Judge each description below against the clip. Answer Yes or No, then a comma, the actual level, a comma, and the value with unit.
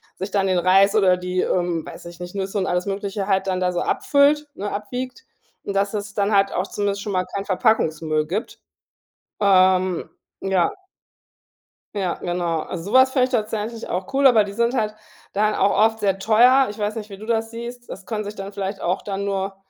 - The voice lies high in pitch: Yes, high, 200 Hz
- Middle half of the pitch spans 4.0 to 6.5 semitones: No, average, 2.8 semitones